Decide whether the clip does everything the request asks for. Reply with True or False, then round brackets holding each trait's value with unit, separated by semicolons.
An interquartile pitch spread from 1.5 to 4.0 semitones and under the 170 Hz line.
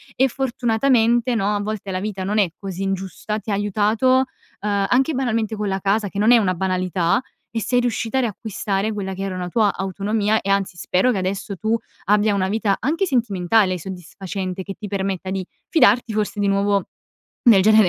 False (2.6 semitones; 205 Hz)